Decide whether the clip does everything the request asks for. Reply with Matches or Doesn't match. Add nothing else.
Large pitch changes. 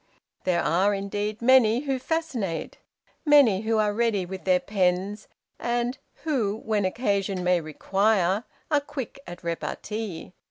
Doesn't match